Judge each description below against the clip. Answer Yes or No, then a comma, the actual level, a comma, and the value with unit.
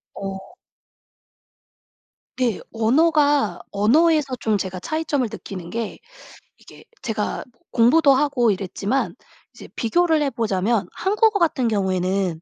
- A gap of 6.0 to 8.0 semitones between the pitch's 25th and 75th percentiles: Yes, wide, 6.9 semitones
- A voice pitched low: No, high, 230 Hz